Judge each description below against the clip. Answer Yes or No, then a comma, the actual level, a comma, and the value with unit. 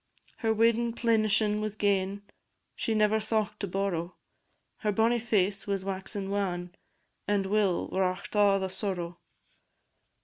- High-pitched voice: Yes, high, 205 Hz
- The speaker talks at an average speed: No, slow, 130 wpm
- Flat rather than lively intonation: Yes, narrow, 2.2 semitones